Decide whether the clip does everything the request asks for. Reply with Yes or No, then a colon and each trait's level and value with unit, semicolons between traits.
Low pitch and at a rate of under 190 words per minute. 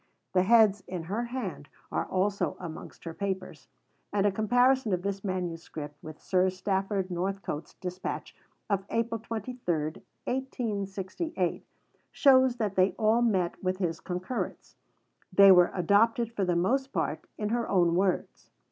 No: high, 195 Hz; average, 140 wpm